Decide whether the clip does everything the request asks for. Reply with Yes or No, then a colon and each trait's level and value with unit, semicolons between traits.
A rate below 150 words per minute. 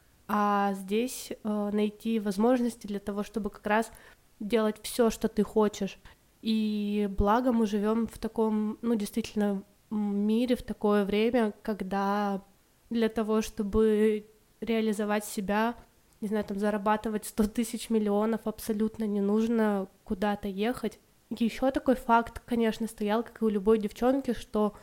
Yes: slow, 135 wpm